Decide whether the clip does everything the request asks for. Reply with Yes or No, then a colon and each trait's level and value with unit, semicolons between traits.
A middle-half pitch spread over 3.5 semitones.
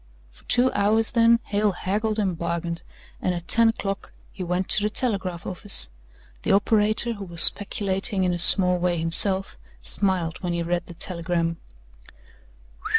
No: average, 3.2 semitones